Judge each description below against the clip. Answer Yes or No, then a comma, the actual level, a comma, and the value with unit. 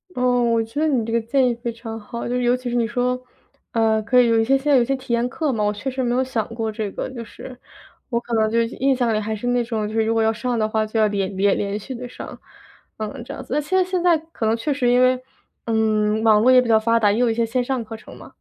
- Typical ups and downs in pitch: No, narrow, 2.3 semitones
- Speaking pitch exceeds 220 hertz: Yes, high, 235 Hz